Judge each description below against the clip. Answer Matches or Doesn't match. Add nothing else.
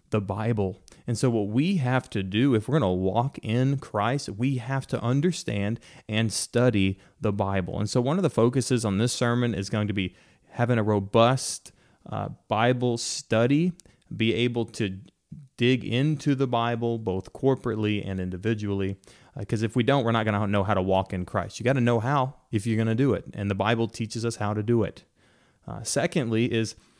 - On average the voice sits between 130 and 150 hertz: Doesn't match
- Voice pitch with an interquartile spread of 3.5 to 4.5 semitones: Matches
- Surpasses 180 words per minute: Matches